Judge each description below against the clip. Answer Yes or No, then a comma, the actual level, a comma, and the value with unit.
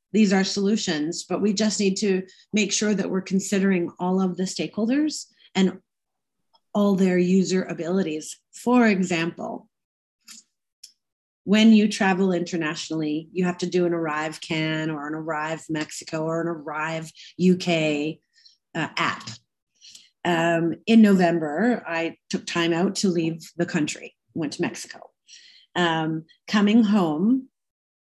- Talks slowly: Yes, slow, 130 wpm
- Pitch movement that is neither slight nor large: Yes, average, 4.0 semitones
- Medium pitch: Yes, medium, 180 Hz